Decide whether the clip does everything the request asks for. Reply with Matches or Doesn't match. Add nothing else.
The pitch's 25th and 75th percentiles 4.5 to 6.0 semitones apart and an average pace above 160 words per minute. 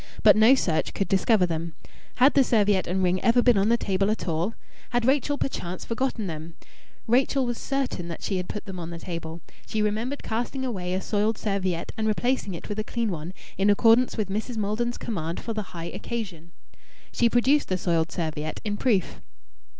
Matches